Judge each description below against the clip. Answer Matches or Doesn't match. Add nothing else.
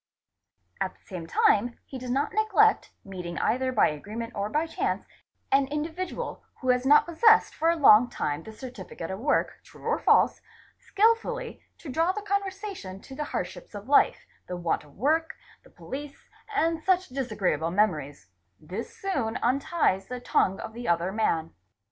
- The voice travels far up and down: Matches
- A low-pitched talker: Doesn't match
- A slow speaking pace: Doesn't match